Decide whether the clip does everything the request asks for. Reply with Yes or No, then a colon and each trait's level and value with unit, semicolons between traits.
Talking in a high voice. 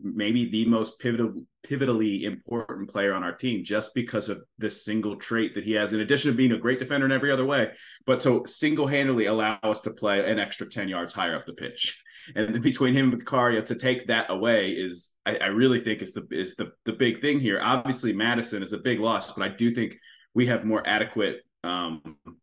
No: low, 115 Hz